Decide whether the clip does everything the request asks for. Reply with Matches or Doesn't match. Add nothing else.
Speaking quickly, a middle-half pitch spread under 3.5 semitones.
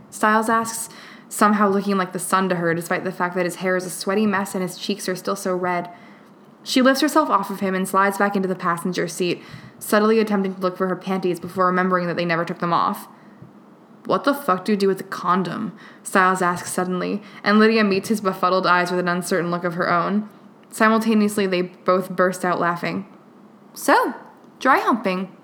Matches